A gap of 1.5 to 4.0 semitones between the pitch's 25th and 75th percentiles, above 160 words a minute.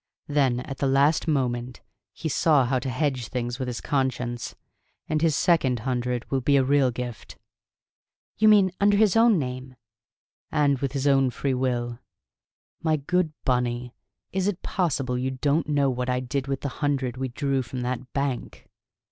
Yes: average, 2.7 semitones; average, 175 wpm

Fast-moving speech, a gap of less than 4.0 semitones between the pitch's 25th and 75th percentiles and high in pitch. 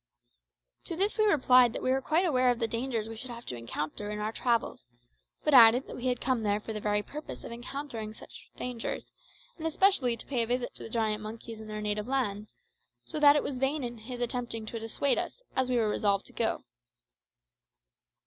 Yes: fast, 215 wpm; average, 3.4 semitones; high, 240 Hz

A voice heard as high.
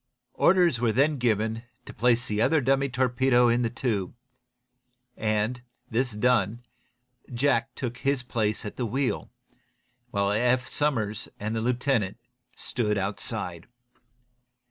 No: low, 120 Hz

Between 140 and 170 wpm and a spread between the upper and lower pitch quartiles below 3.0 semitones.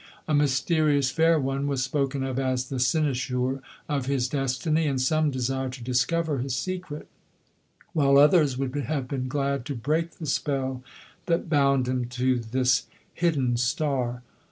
Yes: average, 155 wpm; narrow, 2.6 semitones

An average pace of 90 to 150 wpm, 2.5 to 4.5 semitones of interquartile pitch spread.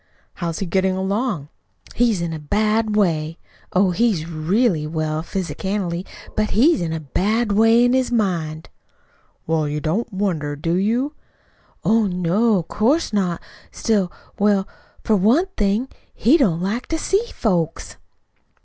No: average, 145 wpm; average, 5.1 semitones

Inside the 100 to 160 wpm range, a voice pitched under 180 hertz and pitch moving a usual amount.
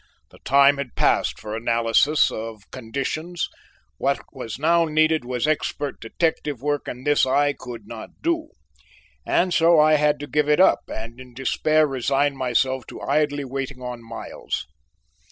Yes: average, 155 wpm; medium, 140 Hz; average, 3.6 semitones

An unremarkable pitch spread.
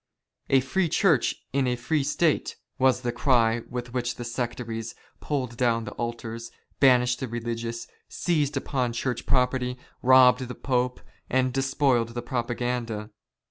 No: narrow, 1.9 semitones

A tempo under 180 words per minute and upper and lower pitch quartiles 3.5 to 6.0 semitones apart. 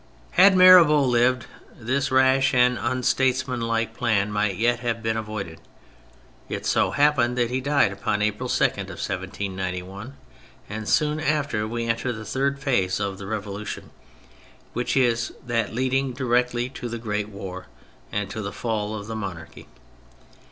Yes: average, 150 wpm; average, 3.8 semitones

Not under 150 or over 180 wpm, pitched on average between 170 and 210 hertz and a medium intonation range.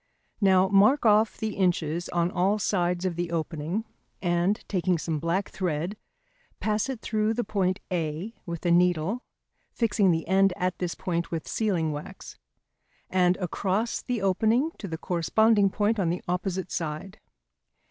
Yes: average, 155 wpm; medium, 185 Hz; average, 3.4 semitones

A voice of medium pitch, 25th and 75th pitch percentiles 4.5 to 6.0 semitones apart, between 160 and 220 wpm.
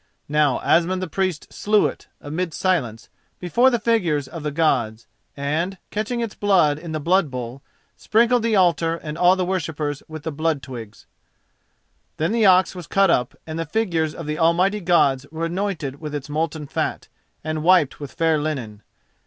No: medium, 165 Hz; average, 4.1 semitones; average, 180 wpm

